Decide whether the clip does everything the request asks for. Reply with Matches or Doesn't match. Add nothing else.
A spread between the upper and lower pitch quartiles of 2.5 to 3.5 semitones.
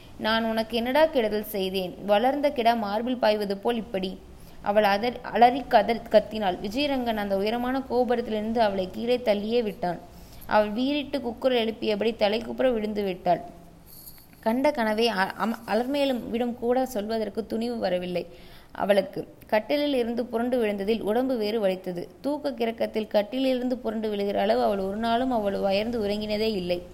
Matches